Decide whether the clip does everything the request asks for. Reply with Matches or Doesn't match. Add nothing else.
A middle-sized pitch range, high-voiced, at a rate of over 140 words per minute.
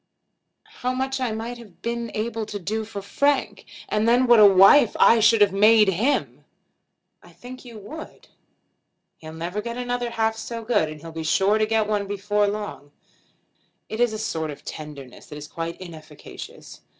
Matches